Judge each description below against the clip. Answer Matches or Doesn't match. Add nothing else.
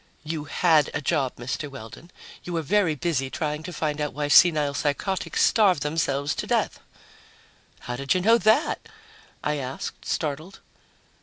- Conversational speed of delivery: Matches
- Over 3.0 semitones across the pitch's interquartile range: Matches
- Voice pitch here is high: Doesn't match